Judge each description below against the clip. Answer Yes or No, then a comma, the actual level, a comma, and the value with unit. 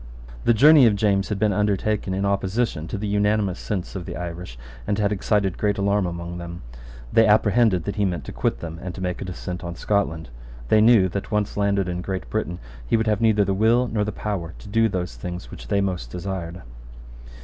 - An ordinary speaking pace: No, fast, 215 wpm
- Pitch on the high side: No, low, 100 Hz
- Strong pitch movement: No, average, 3.0 semitones